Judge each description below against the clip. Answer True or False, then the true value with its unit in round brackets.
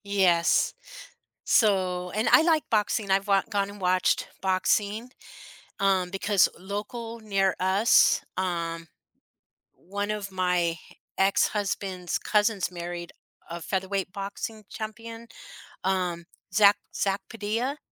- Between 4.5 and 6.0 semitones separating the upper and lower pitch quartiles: False (2.5 semitones)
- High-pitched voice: True (195 Hz)